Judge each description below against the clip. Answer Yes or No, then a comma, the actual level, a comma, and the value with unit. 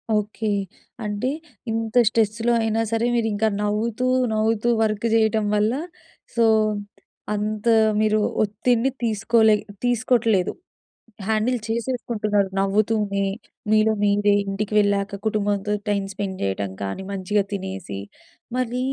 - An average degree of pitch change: No, narrow, 1.8 semitones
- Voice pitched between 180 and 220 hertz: Yes, high, 215 Hz